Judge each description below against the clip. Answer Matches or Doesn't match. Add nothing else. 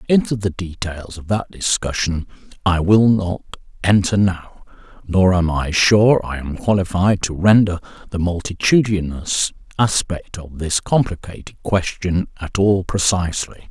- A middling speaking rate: Doesn't match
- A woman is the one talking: Doesn't match